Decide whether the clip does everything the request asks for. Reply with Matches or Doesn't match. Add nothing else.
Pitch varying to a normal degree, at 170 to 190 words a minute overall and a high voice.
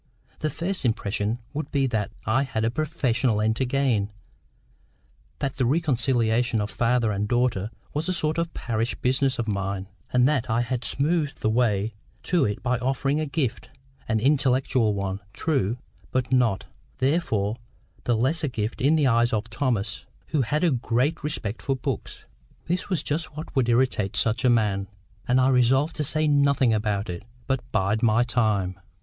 Doesn't match